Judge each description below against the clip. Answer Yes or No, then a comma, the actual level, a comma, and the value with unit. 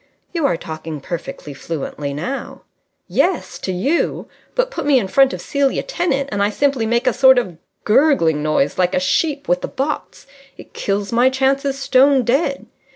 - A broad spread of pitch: Yes, wide, 7.4 semitones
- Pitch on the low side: No, very high, 255 Hz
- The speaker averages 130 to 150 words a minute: No, average, 175 wpm